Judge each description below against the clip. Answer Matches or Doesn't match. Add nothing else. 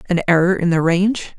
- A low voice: Doesn't match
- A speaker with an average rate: Doesn't match